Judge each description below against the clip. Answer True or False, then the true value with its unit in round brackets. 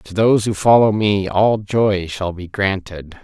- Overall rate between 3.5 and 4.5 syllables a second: True (4.1 syllables/s)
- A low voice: True (100 Hz)